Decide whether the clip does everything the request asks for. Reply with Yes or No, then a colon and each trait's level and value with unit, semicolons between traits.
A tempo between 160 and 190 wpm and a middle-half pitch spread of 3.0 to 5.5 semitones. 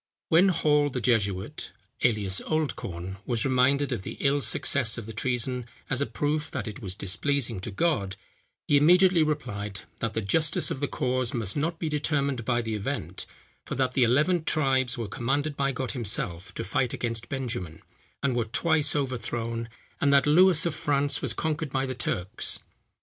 Yes: average, 175 wpm; average, 4.4 semitones